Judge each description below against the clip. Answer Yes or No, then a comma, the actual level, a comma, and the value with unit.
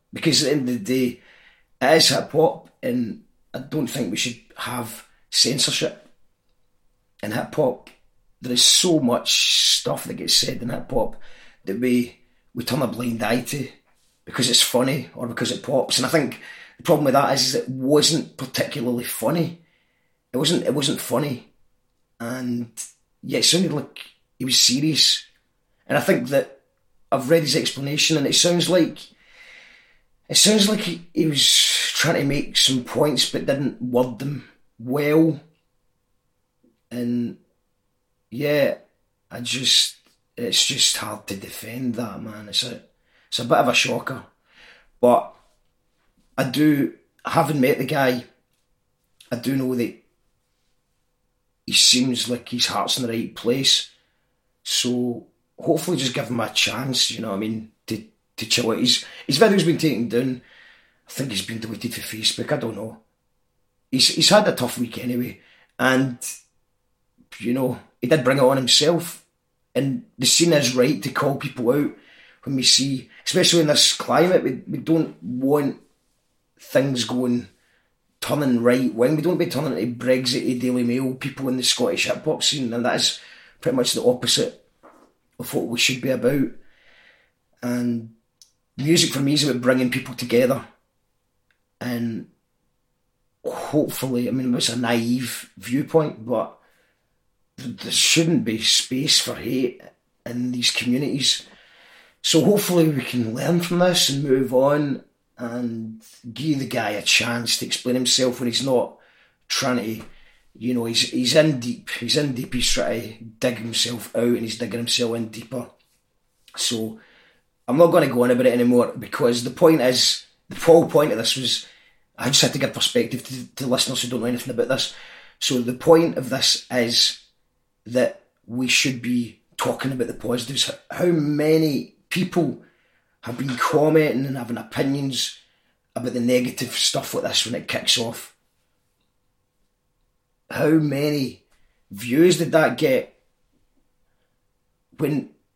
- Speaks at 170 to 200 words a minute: No, average, 160 wpm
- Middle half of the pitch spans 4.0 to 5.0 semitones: No, average, 3.5 semitones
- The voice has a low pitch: Yes, low, 125 Hz